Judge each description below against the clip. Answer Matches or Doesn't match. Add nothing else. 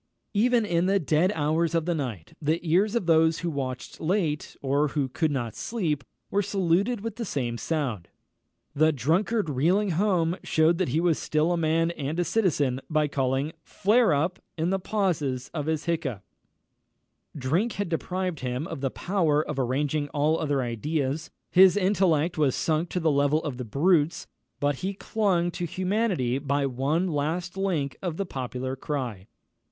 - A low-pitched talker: Doesn't match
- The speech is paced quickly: Doesn't match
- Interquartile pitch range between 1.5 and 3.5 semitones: Doesn't match